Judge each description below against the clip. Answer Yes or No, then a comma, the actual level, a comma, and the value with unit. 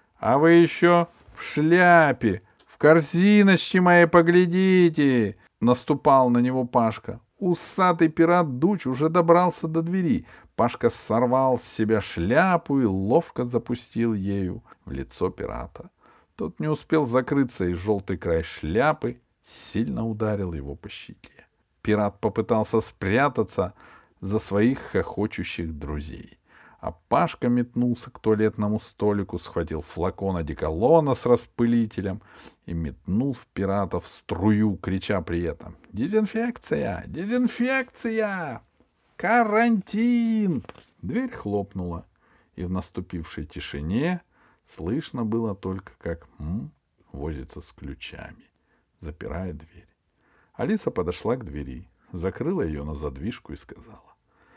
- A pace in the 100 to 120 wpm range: Yes, slow, 110 wpm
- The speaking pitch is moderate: No, low, 115 Hz